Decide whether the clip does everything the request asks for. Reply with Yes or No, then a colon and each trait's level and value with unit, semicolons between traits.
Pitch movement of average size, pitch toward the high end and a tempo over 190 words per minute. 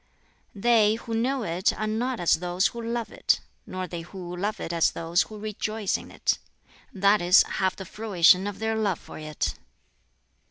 No: average, 3.8 semitones; high, 200 Hz; average, 185 wpm